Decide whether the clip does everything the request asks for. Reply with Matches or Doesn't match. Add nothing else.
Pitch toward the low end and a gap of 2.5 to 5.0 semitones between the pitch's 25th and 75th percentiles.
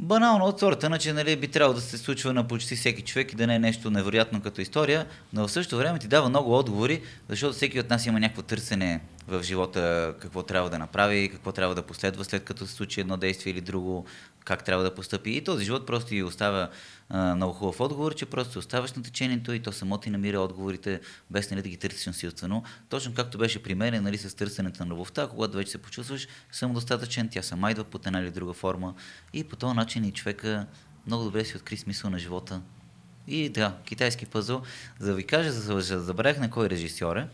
Matches